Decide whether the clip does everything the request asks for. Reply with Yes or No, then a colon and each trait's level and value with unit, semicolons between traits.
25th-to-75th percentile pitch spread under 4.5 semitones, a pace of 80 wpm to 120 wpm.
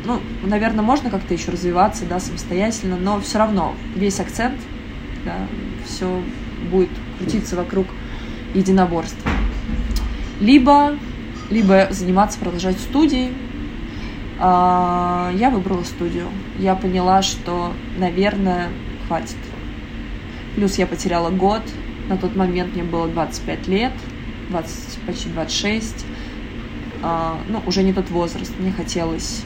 Yes: average, 2.7 semitones; slow, 110 wpm